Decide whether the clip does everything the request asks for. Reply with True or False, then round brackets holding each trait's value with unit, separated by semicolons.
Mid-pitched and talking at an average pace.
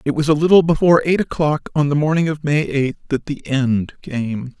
False (145 Hz; 220 wpm)